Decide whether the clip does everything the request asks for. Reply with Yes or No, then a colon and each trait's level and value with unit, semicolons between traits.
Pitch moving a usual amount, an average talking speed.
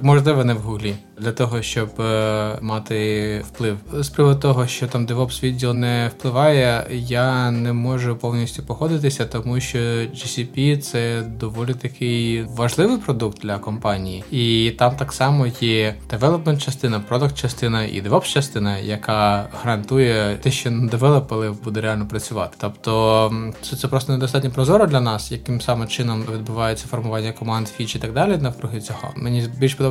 No: average, 3.0 semitones; fast, 160 wpm